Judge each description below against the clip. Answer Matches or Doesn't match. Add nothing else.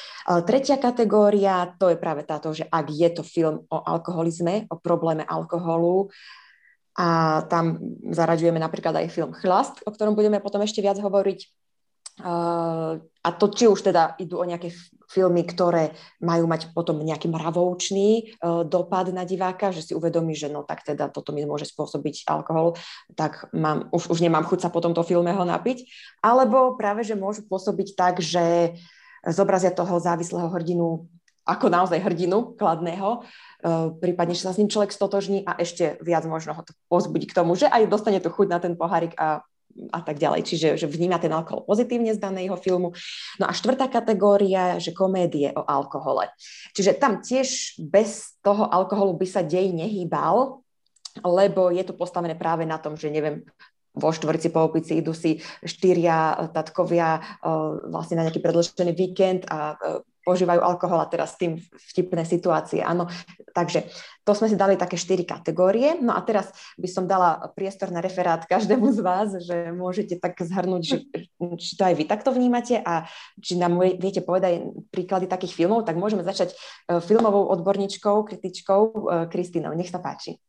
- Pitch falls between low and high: Matches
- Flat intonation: Doesn't match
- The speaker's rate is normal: Doesn't match